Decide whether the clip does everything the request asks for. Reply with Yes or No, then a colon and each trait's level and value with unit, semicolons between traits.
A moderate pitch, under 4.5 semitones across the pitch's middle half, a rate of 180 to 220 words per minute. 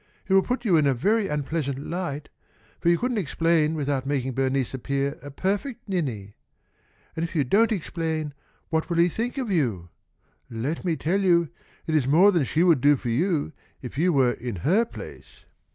No: medium, 160 Hz; average, 5.0 semitones; average, 190 wpm